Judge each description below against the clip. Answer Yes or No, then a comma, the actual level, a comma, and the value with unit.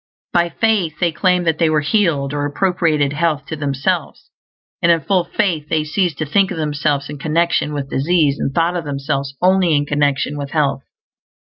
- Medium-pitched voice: Yes, medium, 155 Hz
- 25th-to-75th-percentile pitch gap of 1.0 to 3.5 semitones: Yes, average, 3.0 semitones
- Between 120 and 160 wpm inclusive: No, average, 185 wpm